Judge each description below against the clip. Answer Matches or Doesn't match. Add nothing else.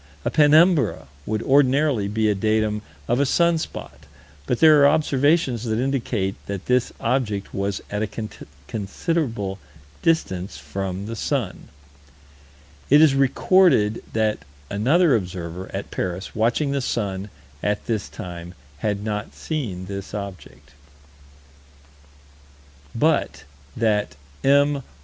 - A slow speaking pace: Matches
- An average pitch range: Doesn't match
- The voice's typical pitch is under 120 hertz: Matches